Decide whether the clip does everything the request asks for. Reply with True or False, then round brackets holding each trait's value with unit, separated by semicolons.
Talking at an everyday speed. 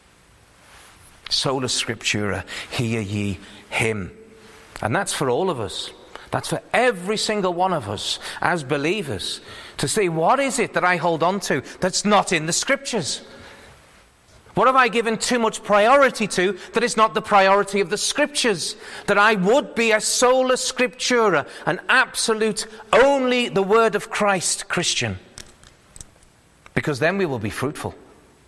True (150 wpm)